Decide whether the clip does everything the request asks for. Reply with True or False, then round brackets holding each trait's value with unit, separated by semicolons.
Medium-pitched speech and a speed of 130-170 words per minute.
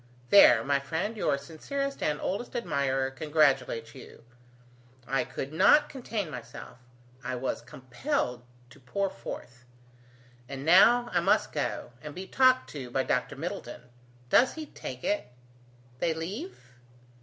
True (150 Hz; 140 wpm)